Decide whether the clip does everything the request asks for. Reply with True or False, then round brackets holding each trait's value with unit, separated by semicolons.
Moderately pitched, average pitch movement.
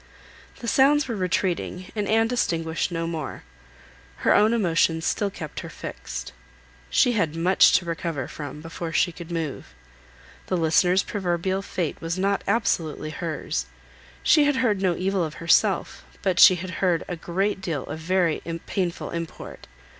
True (175 Hz; 3.2 semitones)